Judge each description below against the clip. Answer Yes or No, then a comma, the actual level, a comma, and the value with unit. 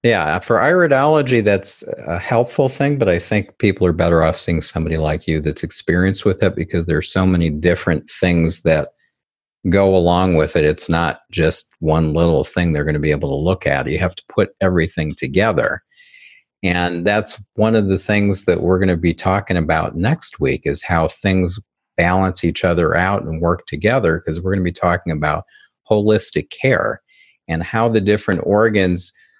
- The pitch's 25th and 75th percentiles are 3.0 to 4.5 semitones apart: Yes, average, 4.0 semitones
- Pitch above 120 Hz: No, very low, 90 Hz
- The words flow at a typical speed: Yes, average, 190 wpm